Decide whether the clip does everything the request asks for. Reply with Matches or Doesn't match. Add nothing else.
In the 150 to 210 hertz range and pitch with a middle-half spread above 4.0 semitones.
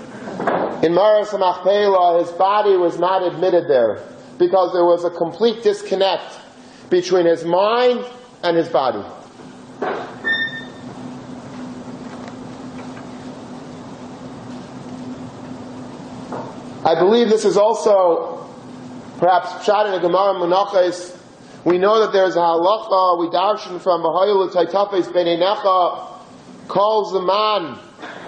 Doesn't match